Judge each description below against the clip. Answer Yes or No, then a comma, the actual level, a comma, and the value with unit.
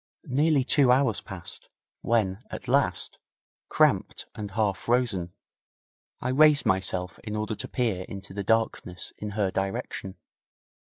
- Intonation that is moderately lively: Yes, average, 4.6 semitones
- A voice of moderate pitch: No, low, 105 Hz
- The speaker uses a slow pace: Yes, slow, 130 wpm